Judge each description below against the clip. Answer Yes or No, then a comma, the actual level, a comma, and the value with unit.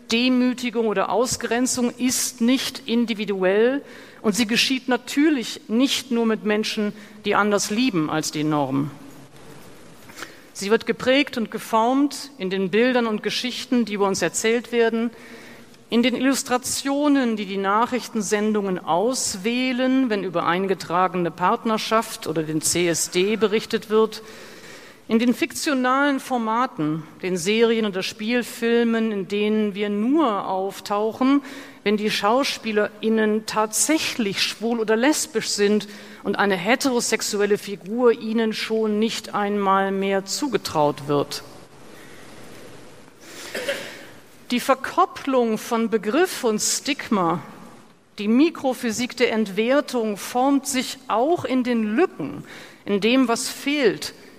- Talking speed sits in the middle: No, slow, 115 wpm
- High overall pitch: Yes, high, 225 Hz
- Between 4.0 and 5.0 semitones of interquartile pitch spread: No, average, 3.3 semitones